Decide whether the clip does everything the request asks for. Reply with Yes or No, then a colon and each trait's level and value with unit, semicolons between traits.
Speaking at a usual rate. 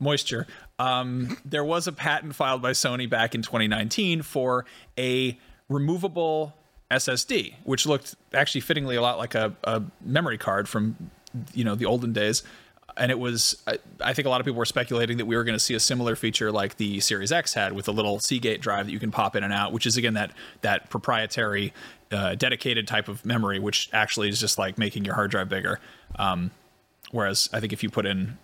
No: fast, 210 wpm